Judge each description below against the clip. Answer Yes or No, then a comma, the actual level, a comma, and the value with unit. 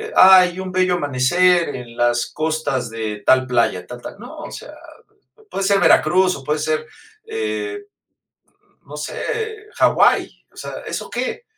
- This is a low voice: No, medium, 175 Hz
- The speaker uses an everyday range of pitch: No, wide, 7.6 semitones